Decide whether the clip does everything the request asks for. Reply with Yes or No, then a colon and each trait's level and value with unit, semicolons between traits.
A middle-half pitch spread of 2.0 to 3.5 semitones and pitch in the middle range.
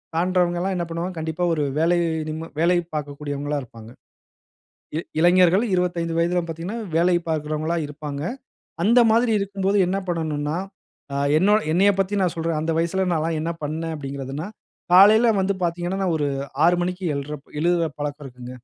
Yes: average, 3.1 semitones; medium, 170 Hz